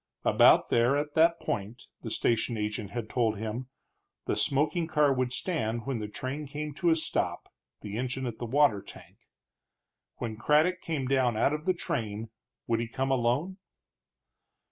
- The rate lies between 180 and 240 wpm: No, average, 165 wpm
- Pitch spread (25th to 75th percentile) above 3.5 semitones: Yes, average, 4.8 semitones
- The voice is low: Yes, low, 130 Hz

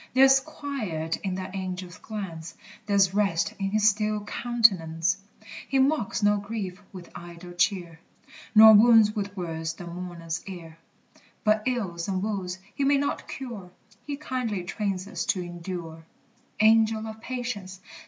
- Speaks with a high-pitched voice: Yes, high, 200 Hz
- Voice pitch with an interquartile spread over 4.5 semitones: No, average, 3.9 semitones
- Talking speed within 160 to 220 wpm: No, average, 145 wpm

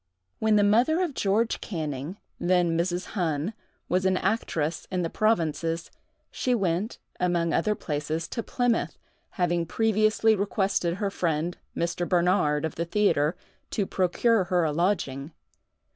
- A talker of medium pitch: Yes, medium, 180 Hz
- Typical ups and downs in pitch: Yes, average, 4.1 semitones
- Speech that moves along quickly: No, average, 140 wpm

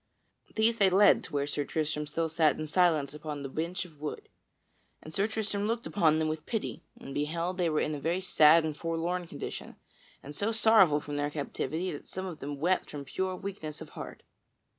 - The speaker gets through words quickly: Yes, fast, 210 wpm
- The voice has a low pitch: No, medium, 160 Hz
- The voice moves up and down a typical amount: Yes, average, 3.8 semitones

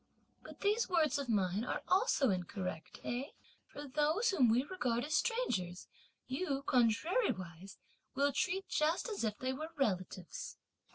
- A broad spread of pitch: Yes, wide, 9.0 semitones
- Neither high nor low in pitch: No, very high, 270 Hz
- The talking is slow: No, average, 145 wpm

